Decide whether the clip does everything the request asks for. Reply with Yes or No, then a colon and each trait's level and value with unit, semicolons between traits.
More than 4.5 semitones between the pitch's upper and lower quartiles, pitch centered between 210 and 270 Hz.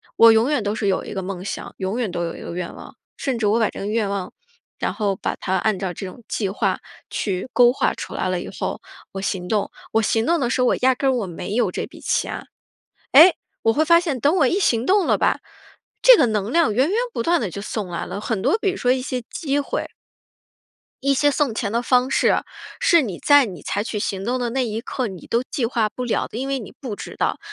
Yes: average, 5.0 semitones; high, 230 Hz